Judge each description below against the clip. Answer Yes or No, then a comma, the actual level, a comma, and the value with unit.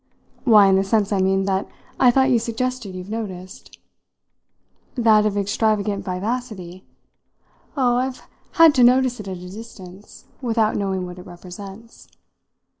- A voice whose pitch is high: Yes, high, 210 Hz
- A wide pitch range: No, average, 3.9 semitones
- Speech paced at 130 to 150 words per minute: Yes, average, 145 wpm